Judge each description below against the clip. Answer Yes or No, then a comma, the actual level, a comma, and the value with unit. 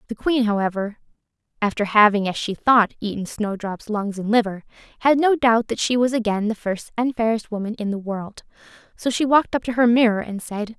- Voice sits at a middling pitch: No, high, 220 Hz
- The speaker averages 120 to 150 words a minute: No, fast, 205 wpm